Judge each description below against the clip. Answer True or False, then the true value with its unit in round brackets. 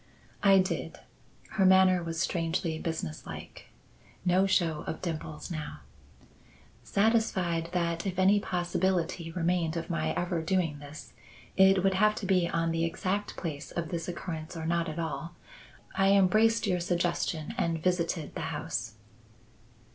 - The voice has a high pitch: False (175 Hz)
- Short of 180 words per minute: True (140 wpm)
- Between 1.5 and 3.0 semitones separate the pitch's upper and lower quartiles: True (2.4 semitones)